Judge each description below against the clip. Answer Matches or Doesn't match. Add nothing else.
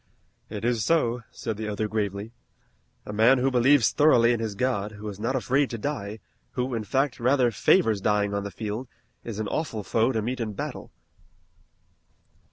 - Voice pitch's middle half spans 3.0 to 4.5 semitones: Matches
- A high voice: Doesn't match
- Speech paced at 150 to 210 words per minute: Matches